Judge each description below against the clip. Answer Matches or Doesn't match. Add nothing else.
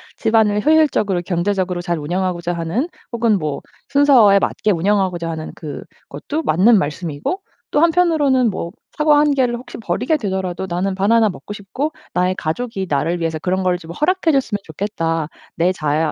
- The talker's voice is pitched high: Matches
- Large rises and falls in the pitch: Matches